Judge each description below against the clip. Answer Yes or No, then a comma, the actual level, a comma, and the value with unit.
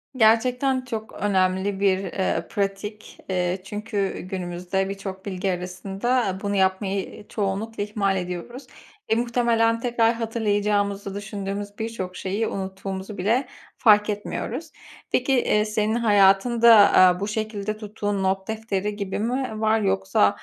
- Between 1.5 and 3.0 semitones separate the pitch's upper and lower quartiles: Yes, narrow, 2.6 semitones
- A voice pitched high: Yes, high, 205 Hz